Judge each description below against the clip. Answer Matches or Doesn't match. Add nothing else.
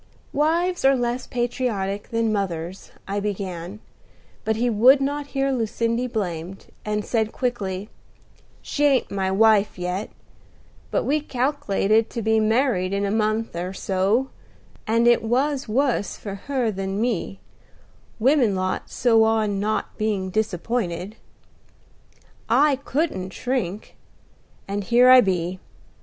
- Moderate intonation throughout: Matches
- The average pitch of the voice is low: Doesn't match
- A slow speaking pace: Matches